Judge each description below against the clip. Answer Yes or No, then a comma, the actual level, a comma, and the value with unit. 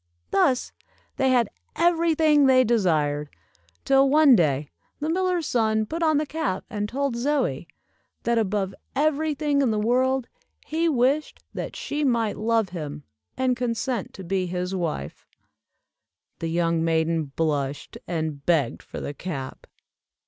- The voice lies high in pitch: Yes, high, 230 Hz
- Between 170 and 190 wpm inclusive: No, average, 145 wpm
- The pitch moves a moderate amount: No, wide, 8.8 semitones